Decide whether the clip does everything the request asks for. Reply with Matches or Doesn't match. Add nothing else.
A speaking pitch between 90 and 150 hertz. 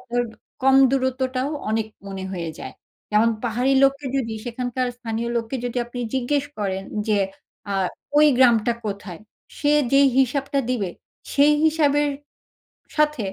Doesn't match